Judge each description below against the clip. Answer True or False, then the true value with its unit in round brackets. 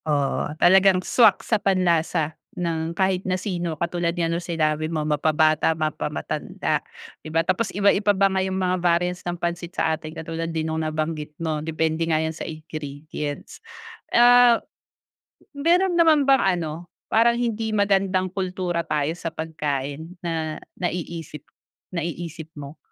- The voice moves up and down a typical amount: True (3.1 semitones)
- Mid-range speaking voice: True (170 Hz)